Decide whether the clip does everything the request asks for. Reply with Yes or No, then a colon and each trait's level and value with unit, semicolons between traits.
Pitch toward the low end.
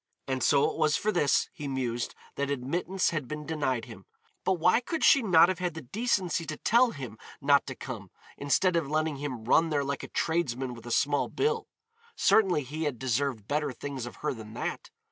No: medium, 145 Hz